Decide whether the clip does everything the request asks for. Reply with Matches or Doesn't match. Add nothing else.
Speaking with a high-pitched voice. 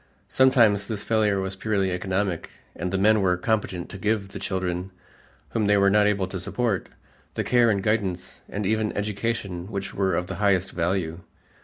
Doesn't match